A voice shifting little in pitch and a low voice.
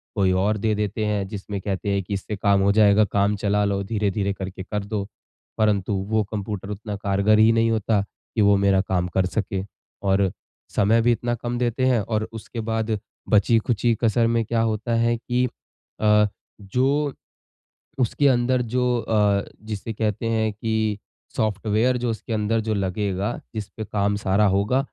Yes: narrow, 2.3 semitones; low, 105 Hz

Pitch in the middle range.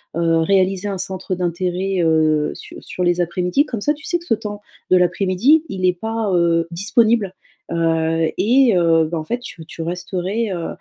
Yes: medium, 180 Hz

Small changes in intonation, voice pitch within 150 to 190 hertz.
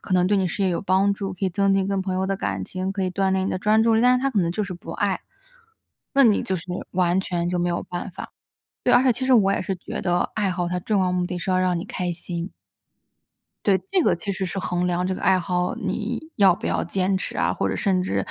Yes: narrow, 1.9 semitones; medium, 185 Hz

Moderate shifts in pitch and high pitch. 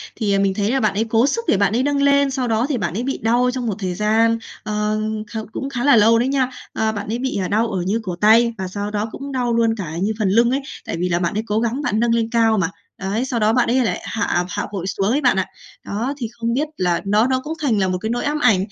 Yes: average, 3.5 semitones; high, 225 Hz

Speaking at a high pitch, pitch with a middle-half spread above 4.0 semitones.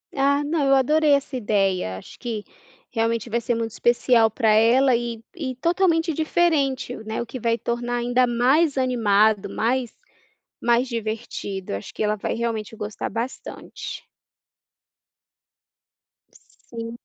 No: high, 235 Hz; average, 3.1 semitones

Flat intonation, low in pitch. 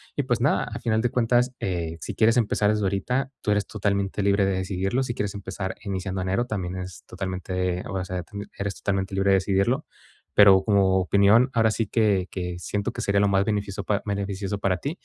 Yes: narrow, 2.3 semitones; low, 100 Hz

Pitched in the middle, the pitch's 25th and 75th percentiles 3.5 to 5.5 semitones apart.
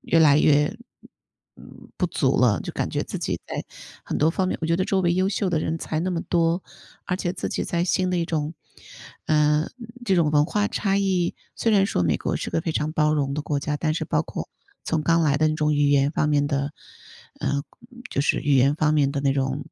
No: medium, 155 Hz; average, 3.1 semitones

